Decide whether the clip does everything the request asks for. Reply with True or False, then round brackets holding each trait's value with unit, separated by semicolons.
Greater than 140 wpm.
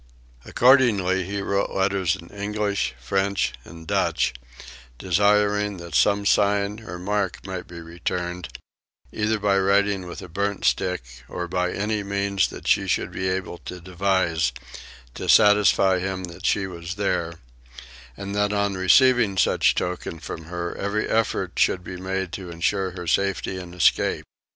True (150 wpm)